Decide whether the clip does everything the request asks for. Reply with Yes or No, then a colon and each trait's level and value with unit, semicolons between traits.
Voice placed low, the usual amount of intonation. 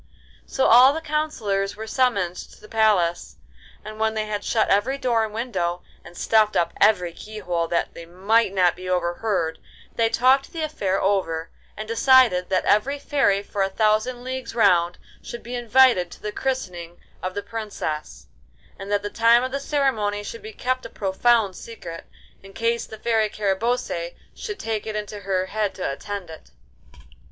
No: high, 215 Hz; average, 4.2 semitones